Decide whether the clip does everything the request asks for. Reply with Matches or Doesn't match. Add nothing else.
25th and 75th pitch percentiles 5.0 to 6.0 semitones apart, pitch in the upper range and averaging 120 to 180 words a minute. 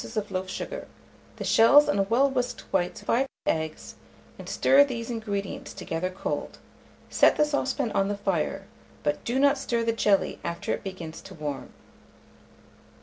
Matches